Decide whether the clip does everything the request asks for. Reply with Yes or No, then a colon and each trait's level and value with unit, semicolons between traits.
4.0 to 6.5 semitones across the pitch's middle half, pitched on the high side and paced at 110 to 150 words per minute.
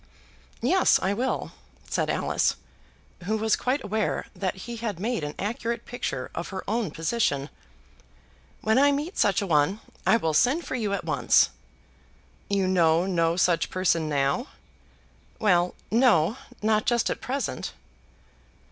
Yes: wide, 5.6 semitones; high, 200 Hz; average, 145 wpm